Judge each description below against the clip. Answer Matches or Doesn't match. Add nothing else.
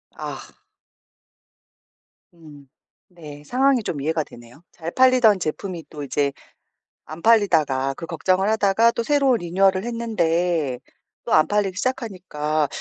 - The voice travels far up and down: Matches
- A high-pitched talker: Doesn't match